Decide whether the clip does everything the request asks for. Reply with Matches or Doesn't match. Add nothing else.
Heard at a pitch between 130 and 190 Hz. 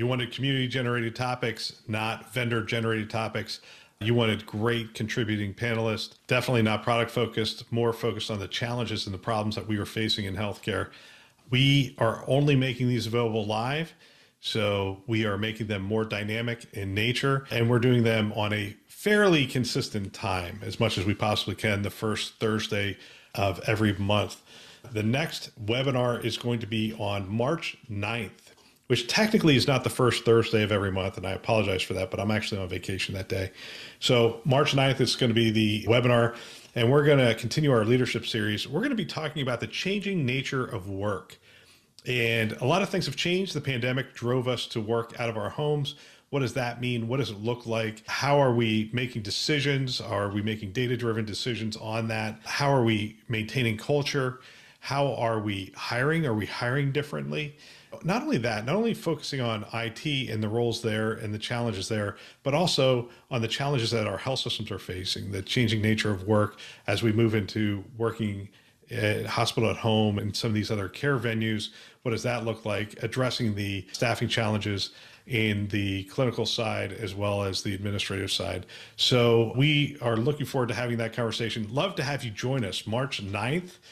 Doesn't match